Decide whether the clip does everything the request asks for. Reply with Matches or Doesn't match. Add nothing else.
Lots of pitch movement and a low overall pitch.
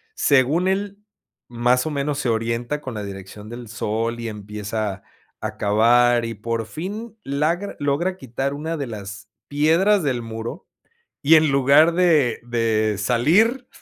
Matches